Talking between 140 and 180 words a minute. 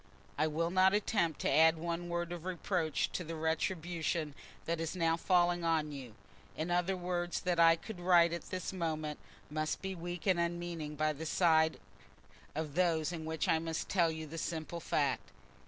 No: average, 190 wpm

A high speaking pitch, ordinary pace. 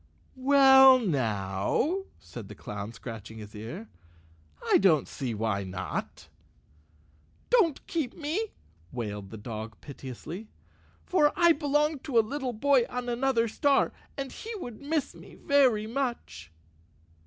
No: high, 235 Hz; slow, 130 wpm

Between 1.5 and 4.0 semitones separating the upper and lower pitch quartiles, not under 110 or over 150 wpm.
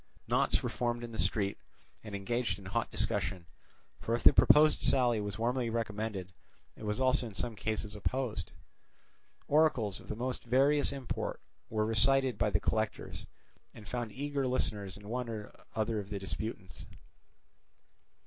No: average, 3.3 semitones; average, 160 wpm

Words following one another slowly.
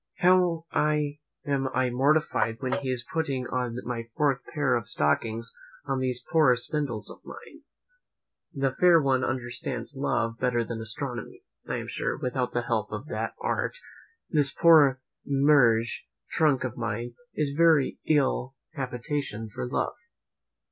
No: average, 150 wpm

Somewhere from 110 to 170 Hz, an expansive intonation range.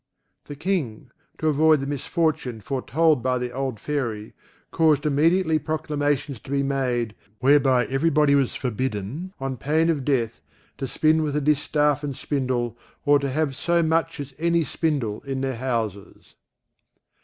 No: medium, 140 Hz; average, 3.2 semitones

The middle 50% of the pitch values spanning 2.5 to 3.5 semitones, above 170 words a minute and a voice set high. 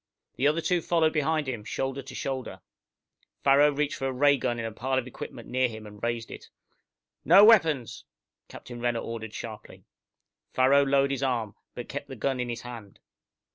No: average, 3.2 semitones; average, 185 wpm; low, 130 Hz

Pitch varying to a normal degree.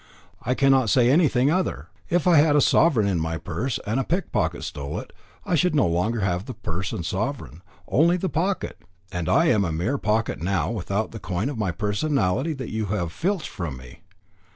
No: wide, 8.2 semitones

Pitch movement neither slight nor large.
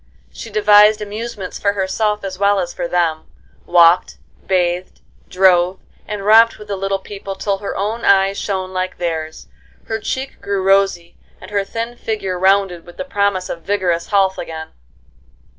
No: narrow, 2.3 semitones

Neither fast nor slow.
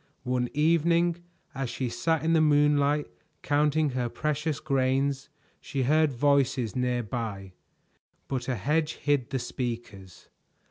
No: slow, 130 wpm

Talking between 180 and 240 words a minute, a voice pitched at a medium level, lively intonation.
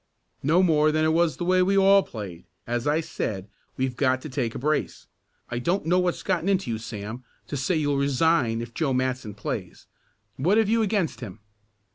Yes: average, 200 wpm; medium, 145 Hz; wide, 6.4 semitones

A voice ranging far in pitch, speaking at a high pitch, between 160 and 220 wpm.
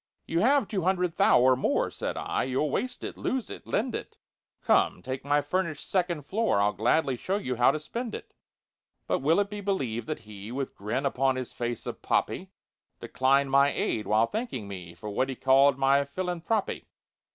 No: wide, 6.6 semitones; medium, 140 Hz; average, 195 wpm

